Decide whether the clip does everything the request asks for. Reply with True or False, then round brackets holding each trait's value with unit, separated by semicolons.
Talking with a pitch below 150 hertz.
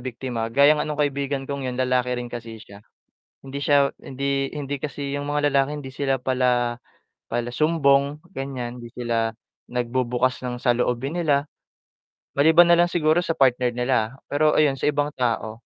True (135 Hz)